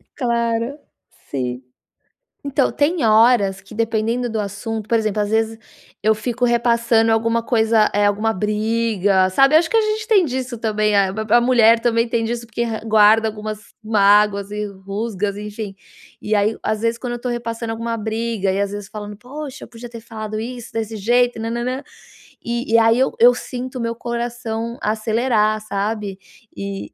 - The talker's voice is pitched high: Yes, high, 225 Hz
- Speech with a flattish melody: Yes, narrow, 2.1 semitones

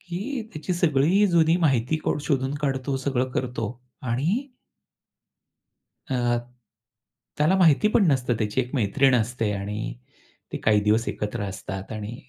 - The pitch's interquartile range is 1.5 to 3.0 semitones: No, wide, 5.6 semitones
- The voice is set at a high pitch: No, low, 130 Hz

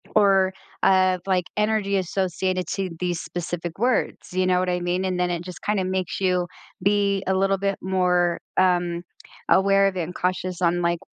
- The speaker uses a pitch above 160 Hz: Yes, medium, 185 Hz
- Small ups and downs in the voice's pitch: Yes, narrow, 1.5 semitones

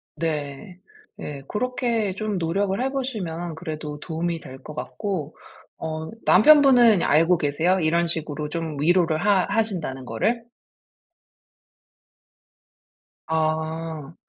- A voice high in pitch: No, medium, 165 Hz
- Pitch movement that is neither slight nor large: Yes, average, 4.3 semitones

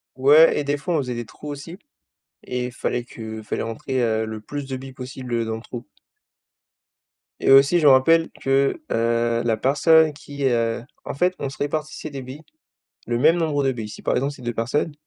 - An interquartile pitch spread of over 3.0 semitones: Yes, average, 3.6 semitones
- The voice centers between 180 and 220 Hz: No, low, 130 Hz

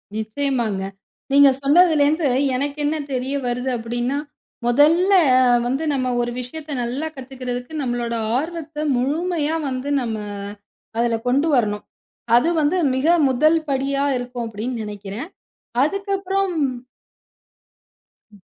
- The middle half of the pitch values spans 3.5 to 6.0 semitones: Yes, average, 4.3 semitones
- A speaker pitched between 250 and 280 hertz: Yes, very high, 270 Hz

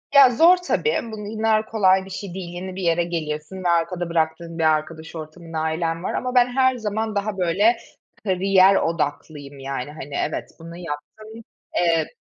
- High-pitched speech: No, medium, 175 Hz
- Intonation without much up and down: No, average, 4.6 semitones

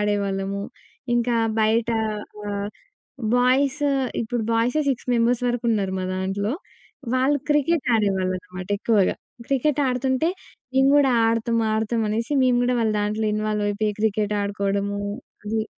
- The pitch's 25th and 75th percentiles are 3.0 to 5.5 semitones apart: Yes, average, 3.5 semitones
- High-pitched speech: Yes, high, 225 Hz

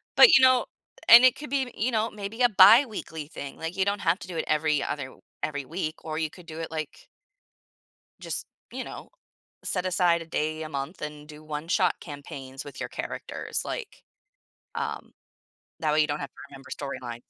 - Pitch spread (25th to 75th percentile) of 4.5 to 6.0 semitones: Yes, average, 5.1 semitones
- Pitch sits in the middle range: Yes, medium, 160 Hz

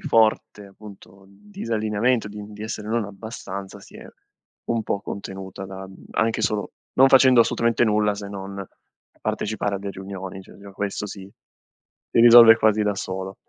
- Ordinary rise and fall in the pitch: No, narrow, 2.1 semitones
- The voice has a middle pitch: No, low, 105 Hz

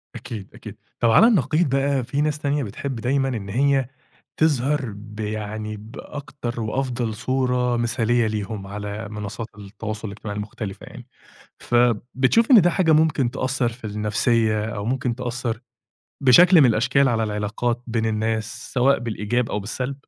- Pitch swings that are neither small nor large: Yes, average, 3.8 semitones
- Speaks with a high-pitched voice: No, low, 120 Hz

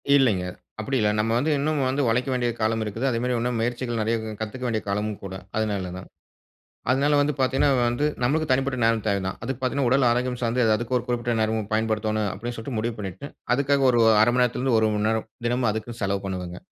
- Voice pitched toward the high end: No, low, 120 Hz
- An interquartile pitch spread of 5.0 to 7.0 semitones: No, average, 2.9 semitones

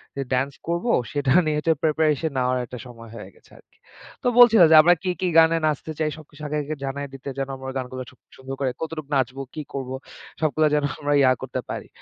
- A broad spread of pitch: No, average, 3.0 semitones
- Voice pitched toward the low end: No, medium, 145 Hz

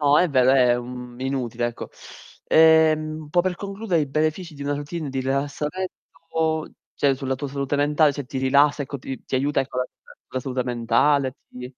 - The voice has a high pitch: No, medium, 140 Hz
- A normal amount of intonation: Yes, average, 3.0 semitones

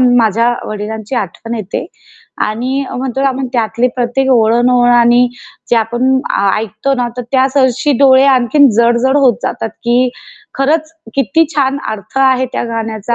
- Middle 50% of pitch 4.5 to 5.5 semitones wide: No, average, 2.7 semitones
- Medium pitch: No, high, 245 Hz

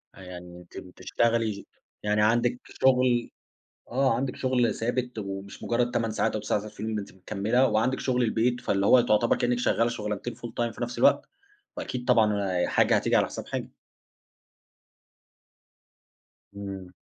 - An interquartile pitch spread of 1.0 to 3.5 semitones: Yes, average, 3.1 semitones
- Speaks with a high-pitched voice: No, low, 115 Hz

